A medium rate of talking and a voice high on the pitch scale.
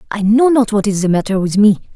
No: fast, 275 wpm; high, 210 Hz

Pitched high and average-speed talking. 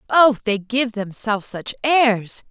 Yes: high, 230 Hz; average, 145 wpm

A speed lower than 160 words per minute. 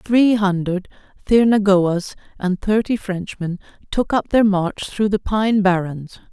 Yes: slow, 135 wpm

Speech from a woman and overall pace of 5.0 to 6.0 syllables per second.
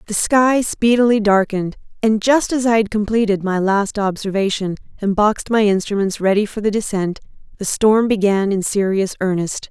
Yes: female; 5.1 syllables/s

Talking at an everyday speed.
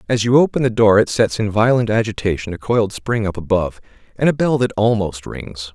No: fast, 220 wpm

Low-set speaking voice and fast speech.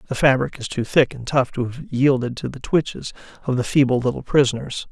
Yes: low, 130 Hz; fast, 220 wpm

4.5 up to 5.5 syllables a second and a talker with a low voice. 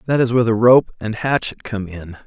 No: 5.7 syllables/s; low, 115 Hz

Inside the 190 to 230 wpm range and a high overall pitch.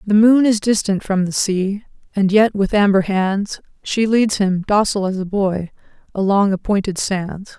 No: average, 175 wpm; high, 200 Hz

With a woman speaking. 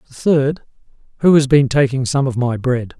No: male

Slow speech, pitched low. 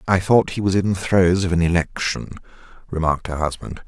No: average, 200 wpm; very low, 90 Hz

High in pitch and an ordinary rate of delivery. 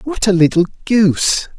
No: medium, 175 Hz; average, 150 wpm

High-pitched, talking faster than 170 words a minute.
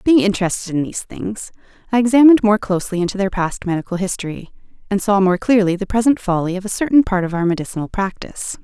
Yes: high, 200 Hz; average, 200 wpm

